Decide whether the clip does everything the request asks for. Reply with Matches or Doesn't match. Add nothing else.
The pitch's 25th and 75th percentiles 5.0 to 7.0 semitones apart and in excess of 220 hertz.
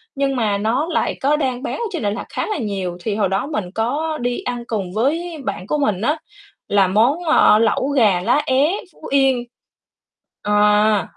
Matches